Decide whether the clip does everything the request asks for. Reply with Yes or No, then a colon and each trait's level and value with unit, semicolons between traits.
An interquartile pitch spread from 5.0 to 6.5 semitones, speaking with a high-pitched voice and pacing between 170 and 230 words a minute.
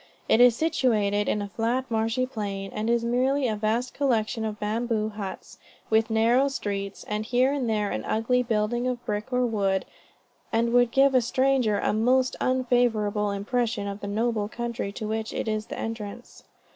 No: average, 2.8 semitones; high, 225 Hz; average, 180 wpm